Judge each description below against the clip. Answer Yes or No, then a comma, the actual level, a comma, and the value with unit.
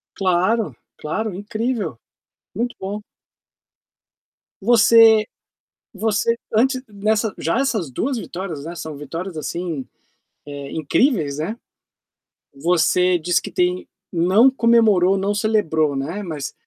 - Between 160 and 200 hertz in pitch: Yes, high, 190 Hz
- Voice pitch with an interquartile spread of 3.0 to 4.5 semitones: No, average, 5.2 semitones